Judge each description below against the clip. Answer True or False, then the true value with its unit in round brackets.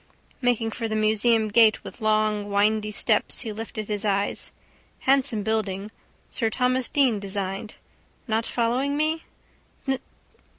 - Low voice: False (220 Hz)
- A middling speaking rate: False (125 wpm)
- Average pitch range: False (2.2 semitones)